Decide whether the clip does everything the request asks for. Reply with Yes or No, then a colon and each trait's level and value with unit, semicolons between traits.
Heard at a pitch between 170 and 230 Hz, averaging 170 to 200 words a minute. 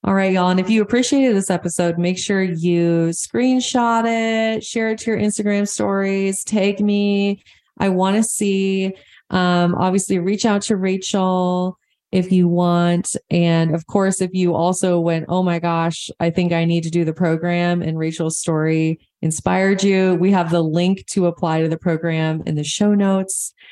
Yes: medium, 185 Hz; average, 180 wpm